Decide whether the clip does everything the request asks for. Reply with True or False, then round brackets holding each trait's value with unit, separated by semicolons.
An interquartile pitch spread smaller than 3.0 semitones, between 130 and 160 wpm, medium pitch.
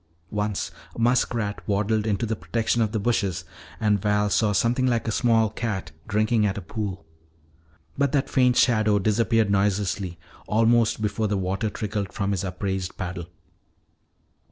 False (2.4 semitones; 155 wpm; 105 Hz)